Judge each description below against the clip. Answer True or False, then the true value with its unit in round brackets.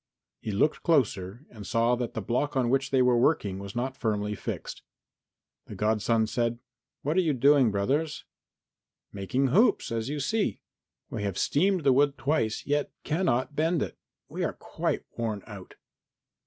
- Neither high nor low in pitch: False (125 Hz)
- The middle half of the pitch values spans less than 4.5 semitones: False (4.9 semitones)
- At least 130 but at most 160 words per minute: False (170 wpm)